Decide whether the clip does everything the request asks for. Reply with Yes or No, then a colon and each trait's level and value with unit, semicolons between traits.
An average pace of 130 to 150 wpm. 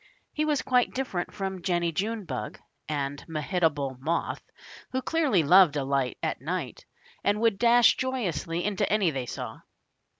Yes: average, 145 wpm